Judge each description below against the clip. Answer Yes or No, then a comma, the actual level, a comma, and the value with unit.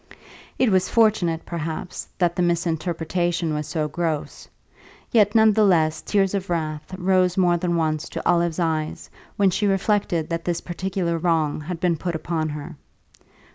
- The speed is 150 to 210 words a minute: Yes, average, 160 wpm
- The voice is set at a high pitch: No, medium, 170 Hz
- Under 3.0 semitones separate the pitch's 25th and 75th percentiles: Yes, narrow, 2.6 semitones